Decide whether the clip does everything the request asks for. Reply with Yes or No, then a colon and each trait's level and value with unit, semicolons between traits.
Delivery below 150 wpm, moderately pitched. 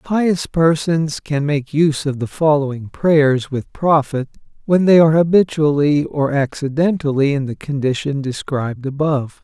Yes: average, 140 wpm; medium, 150 Hz